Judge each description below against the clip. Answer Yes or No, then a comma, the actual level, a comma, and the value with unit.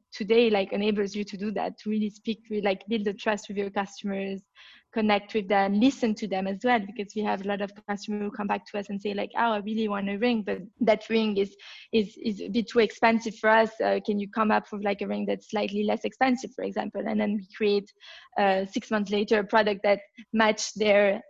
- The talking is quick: Yes, fast, 245 wpm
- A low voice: No, high, 210 Hz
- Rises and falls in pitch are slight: Yes, narrow, 1.6 semitones